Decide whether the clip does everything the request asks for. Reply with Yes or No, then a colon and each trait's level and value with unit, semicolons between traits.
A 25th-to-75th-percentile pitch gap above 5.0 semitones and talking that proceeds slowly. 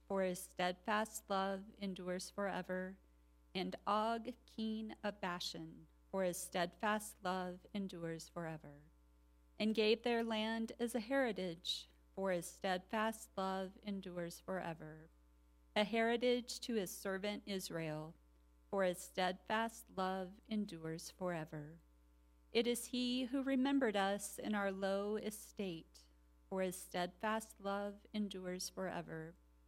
No: average, 4.6 semitones; slow, 115 wpm